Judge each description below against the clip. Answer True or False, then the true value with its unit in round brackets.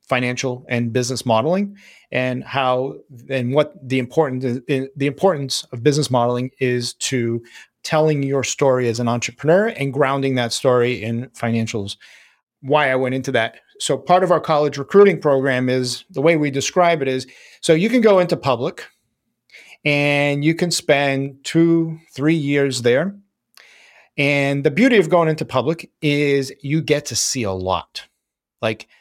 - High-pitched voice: False (140 Hz)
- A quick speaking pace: False (160 wpm)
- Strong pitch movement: False (4.1 semitones)